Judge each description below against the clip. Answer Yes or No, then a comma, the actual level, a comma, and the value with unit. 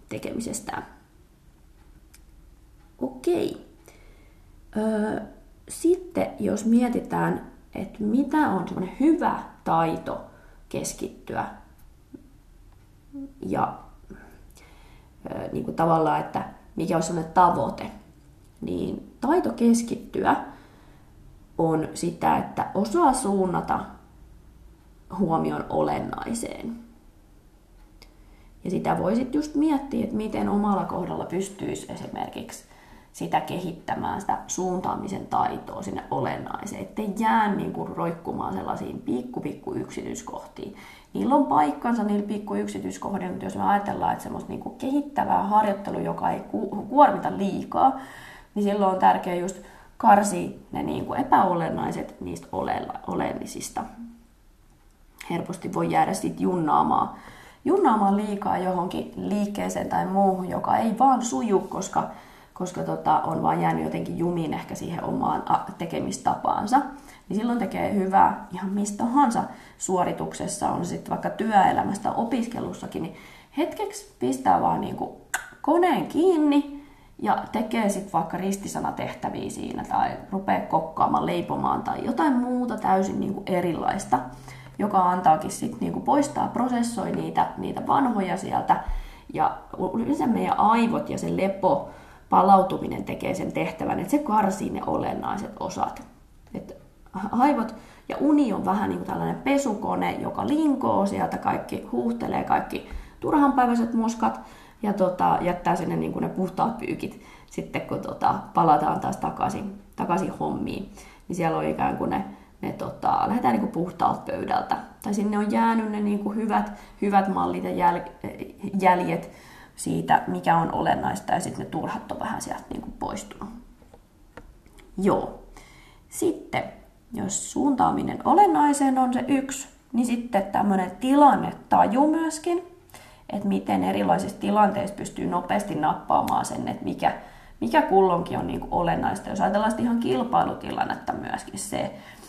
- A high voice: Yes, high, 205 Hz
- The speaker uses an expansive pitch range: Yes, wide, 6.6 semitones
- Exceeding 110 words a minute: Yes, average, 120 wpm